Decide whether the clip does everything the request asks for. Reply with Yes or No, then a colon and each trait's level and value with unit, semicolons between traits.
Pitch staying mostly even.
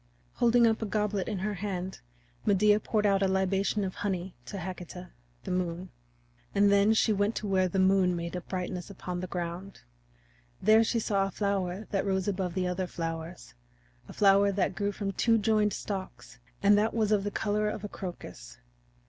Yes: narrow, 2.3 semitones